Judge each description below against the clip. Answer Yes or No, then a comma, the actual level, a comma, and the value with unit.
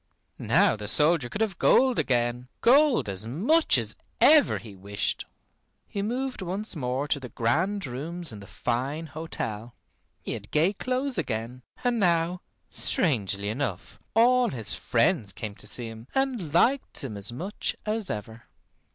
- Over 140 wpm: Yes, average, 155 wpm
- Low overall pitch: No, medium, 150 Hz